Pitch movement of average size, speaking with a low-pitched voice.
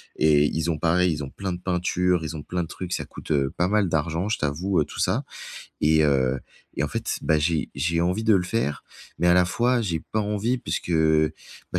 Yes: average, 3.1 semitones; very low, 85 Hz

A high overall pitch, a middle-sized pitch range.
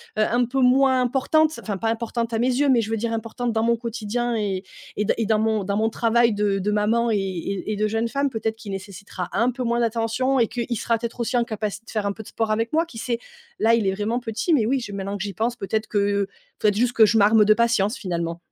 No: high, 225 Hz; narrow, 2.3 semitones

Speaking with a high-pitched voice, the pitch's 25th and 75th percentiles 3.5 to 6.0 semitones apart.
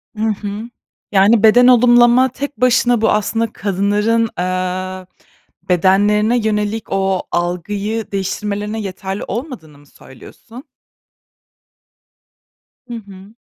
No: high, 210 Hz; average, 3.0 semitones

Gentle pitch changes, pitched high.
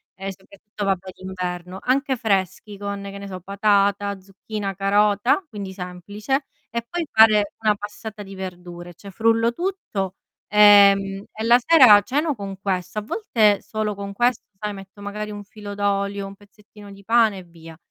Yes: narrow, 1.8 semitones; high, 205 Hz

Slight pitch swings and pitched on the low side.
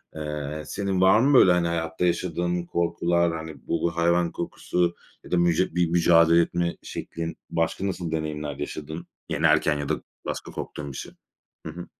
Yes: narrow, 1.7 semitones; very low, 85 Hz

